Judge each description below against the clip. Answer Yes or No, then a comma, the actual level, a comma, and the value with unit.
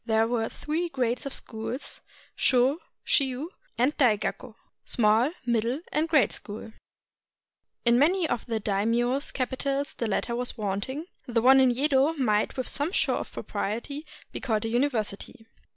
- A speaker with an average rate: Yes, average, 150 wpm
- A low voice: No, high, 245 Hz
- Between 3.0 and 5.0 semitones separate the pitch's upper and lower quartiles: Yes, average, 3.8 semitones